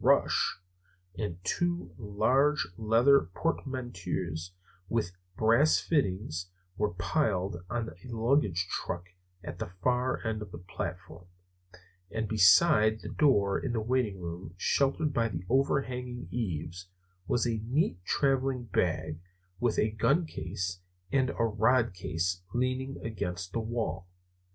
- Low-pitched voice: Yes, low, 110 Hz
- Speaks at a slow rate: Yes, slow, 125 wpm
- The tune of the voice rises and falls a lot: Yes, wide, 5.8 semitones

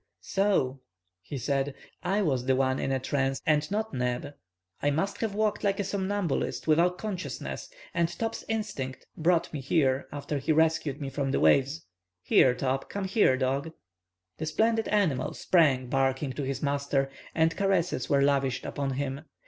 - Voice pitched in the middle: Yes, medium, 145 Hz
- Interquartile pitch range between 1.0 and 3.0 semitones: No, average, 5.1 semitones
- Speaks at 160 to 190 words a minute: Yes, average, 165 wpm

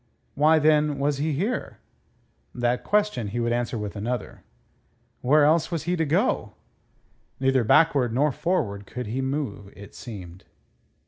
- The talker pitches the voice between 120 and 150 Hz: Yes, low, 135 Hz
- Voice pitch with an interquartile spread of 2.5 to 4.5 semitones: No, average, 4.9 semitones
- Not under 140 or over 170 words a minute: Yes, average, 145 wpm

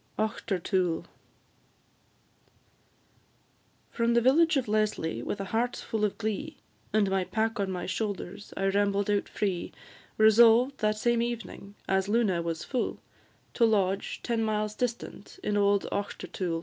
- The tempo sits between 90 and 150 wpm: Yes, slow, 135 wpm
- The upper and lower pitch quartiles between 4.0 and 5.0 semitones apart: No, average, 3.0 semitones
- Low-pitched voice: No, high, 210 Hz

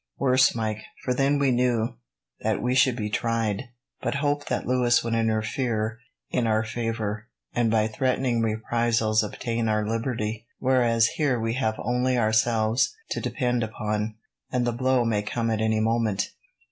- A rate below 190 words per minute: Yes, average, 160 wpm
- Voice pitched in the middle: No, low, 115 Hz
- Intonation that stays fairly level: Yes, narrow, 2.3 semitones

